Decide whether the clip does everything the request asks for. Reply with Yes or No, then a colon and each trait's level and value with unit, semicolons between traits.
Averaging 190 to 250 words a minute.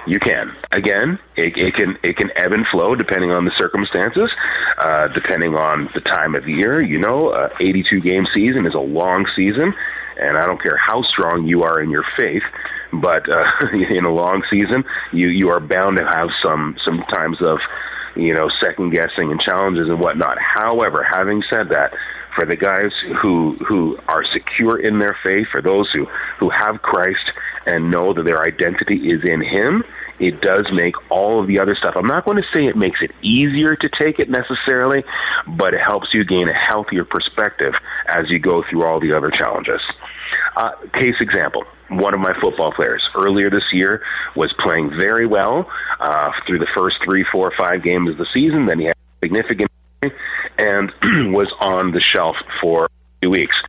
Yes: average, 195 wpm